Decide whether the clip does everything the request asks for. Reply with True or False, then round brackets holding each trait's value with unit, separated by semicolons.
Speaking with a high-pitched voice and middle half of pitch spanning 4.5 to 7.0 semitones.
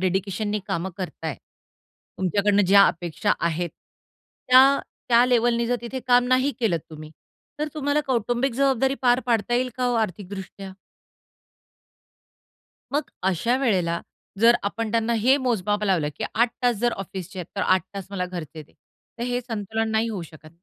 True (215 Hz; 4.8 semitones)